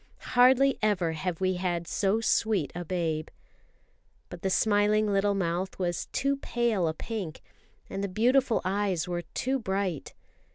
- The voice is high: Yes, high, 195 Hz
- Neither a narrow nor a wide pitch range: Yes, average, 3.9 semitones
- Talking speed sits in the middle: Yes, average, 150 wpm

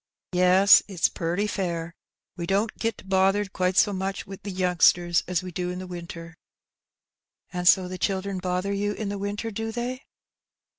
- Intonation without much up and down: Yes, narrow, 2.1 semitones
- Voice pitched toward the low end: No, high, 190 Hz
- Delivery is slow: No, average, 170 wpm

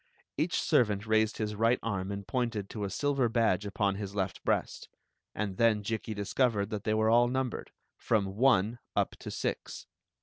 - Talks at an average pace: Yes, average, 180 wpm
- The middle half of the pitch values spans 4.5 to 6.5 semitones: No, narrow, 2.6 semitones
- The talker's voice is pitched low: Yes, low, 110 Hz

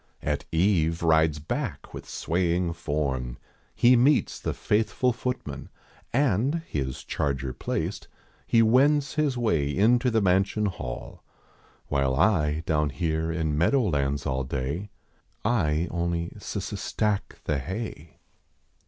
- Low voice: Yes, very low, 85 Hz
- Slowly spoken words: Yes, slow, 125 wpm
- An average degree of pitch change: No, wide, 6.9 semitones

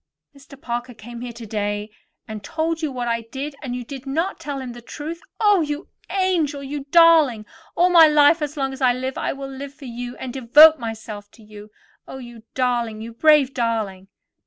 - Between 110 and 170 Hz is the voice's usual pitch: No, very high, 265 Hz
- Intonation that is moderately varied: Yes, average, 4.2 semitones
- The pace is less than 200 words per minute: No, fast, 205 wpm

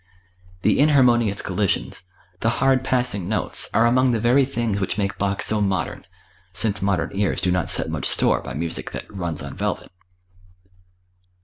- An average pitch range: Yes, average, 4.0 semitones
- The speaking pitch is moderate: No, low, 105 Hz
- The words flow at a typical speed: Yes, average, 165 wpm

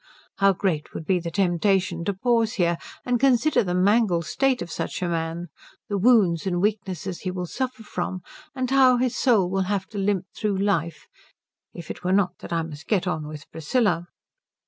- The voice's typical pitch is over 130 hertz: Yes, high, 190 Hz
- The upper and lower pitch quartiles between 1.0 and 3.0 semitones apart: No, average, 4.1 semitones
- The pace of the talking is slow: No, average, 190 wpm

